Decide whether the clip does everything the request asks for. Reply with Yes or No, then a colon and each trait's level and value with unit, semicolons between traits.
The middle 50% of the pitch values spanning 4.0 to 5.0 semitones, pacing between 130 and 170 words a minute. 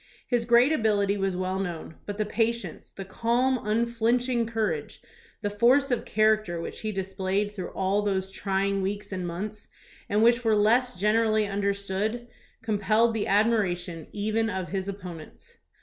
No: average, 2.9 semitones; average, 160 wpm